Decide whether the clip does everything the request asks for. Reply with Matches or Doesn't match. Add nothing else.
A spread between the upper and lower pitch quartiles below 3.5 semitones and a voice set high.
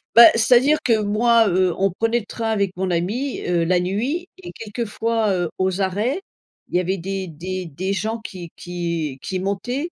Doesn't match